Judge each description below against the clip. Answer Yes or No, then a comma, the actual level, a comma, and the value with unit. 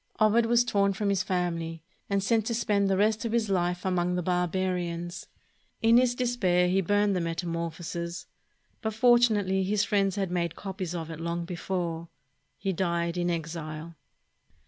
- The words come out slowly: No, average, 165 wpm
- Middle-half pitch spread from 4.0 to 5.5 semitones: No, average, 3.2 semitones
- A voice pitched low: No, medium, 185 Hz